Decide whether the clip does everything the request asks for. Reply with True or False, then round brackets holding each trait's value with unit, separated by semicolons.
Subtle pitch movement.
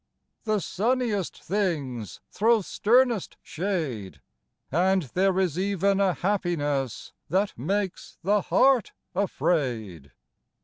False (5.3 semitones)